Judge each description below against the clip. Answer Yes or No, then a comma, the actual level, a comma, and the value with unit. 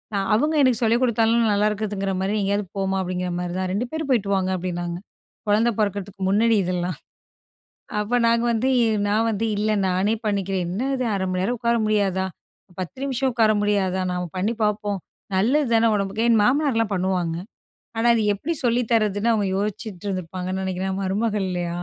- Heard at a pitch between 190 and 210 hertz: Yes, high, 205 Hz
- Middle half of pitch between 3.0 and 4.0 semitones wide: Yes, average, 3.4 semitones